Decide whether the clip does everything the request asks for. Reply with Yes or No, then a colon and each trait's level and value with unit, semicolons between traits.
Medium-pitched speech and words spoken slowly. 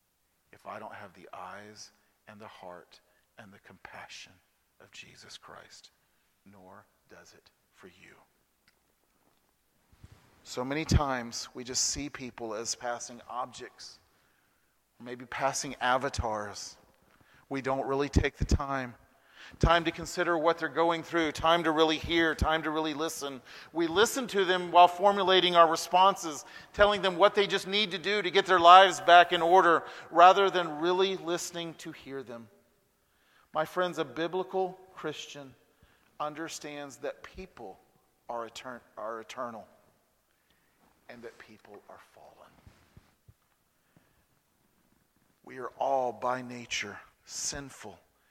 Yes: medium, 160 Hz; slow, 130 wpm